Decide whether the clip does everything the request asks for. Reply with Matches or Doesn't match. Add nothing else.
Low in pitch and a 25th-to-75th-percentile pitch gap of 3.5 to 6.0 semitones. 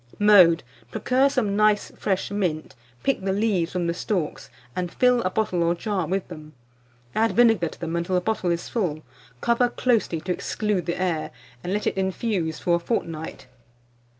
Doesn't match